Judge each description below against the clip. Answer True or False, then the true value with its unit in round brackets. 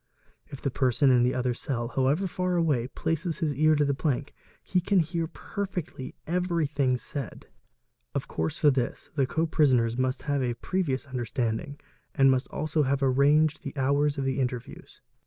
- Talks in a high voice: False (140 Hz)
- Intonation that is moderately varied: True (3.4 semitones)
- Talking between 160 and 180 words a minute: True (175 wpm)